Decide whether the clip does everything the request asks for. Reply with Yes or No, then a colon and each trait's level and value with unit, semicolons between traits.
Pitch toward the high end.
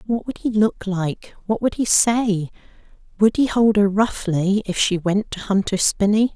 Yes: high, 205 Hz